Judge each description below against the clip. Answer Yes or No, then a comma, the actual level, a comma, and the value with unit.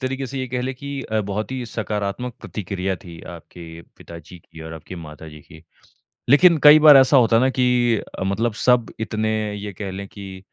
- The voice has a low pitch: Yes, low, 110 Hz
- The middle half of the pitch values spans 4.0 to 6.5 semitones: Yes, average, 5.1 semitones